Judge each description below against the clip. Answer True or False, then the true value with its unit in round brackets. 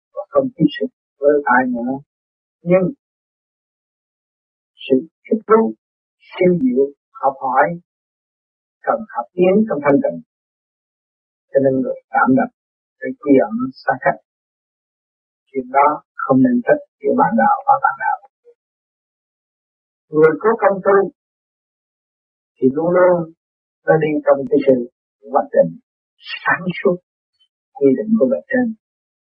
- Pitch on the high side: False (180 Hz)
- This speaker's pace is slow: True (125 wpm)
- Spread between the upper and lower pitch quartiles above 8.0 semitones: True (8.8 semitones)